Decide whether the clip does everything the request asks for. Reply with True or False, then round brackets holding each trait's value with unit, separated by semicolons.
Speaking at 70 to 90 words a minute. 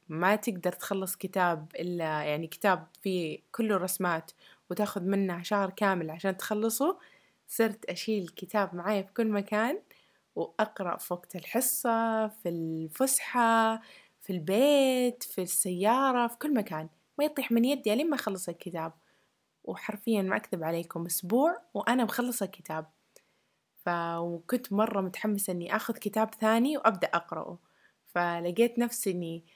False (130 wpm)